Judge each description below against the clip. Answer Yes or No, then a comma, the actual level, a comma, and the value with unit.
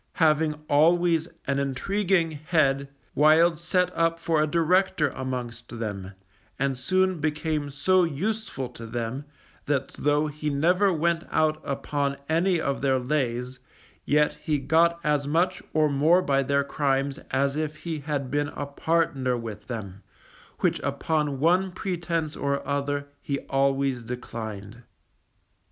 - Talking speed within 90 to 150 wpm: Yes, average, 140 wpm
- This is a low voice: No, medium, 145 Hz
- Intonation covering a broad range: No, average, 3.4 semitones